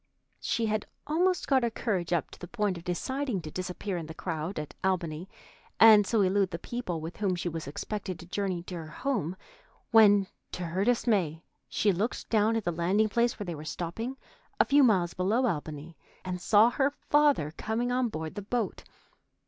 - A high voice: Yes, high, 195 Hz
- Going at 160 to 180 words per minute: No, average, 195 wpm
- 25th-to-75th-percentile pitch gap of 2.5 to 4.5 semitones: No, average, 5.0 semitones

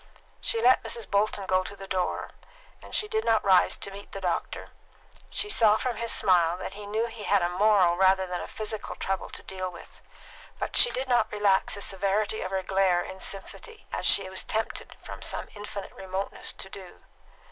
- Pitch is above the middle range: Yes, high, 195 Hz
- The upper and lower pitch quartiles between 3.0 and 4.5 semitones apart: No, narrow, 2.4 semitones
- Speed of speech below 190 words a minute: No, average, 200 wpm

